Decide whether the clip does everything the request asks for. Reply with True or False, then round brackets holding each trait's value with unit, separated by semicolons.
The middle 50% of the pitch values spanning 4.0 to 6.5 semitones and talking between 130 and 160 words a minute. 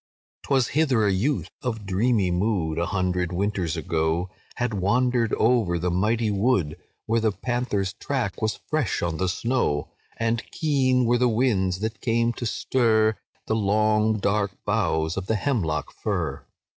True (4.5 semitones; 155 wpm)